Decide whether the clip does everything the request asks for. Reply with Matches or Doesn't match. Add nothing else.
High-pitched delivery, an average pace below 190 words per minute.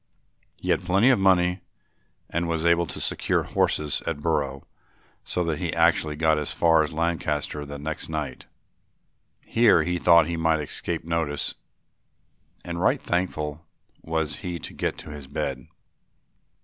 Doesn't match